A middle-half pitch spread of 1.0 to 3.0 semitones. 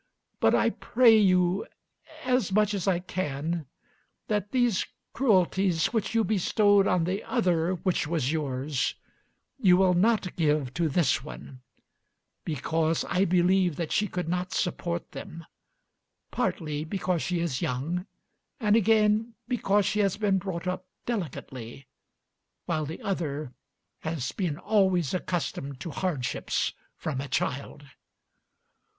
No: average, 4.2 semitones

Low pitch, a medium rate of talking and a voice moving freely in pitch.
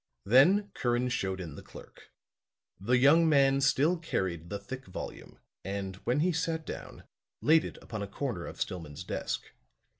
Yes: low, 125 Hz; average, 160 wpm; wide, 7.8 semitones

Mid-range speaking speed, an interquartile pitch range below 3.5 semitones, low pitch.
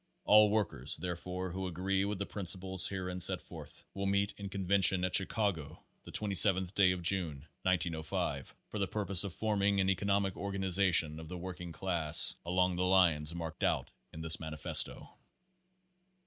Yes: average, 165 wpm; narrow, 2.5 semitones; very low, 90 Hz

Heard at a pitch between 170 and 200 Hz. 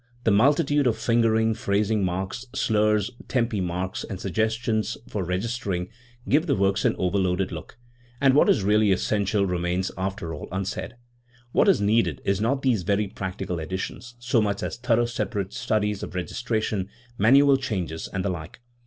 No: low, 105 Hz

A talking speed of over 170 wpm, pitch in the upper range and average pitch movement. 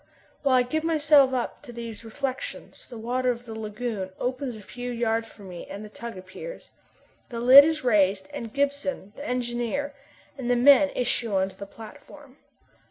Yes: average, 180 wpm; high, 245 Hz; average, 3.8 semitones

